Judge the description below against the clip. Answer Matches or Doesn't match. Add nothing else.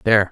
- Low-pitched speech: Matches